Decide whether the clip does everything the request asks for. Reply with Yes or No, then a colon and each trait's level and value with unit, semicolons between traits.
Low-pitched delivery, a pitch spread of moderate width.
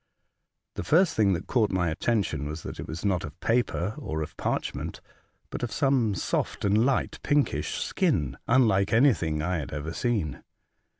No: low, 100 Hz; wide, 7.1 semitones